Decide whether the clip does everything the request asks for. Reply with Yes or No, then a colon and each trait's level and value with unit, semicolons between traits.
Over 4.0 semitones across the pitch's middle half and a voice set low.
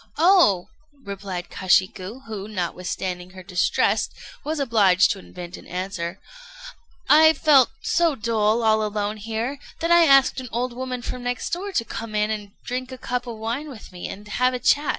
No: average, 4.9 semitones; high, 225 Hz